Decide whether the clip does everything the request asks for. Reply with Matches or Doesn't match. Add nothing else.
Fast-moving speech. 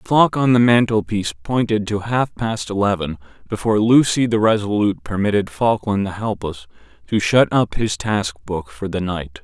Doesn't match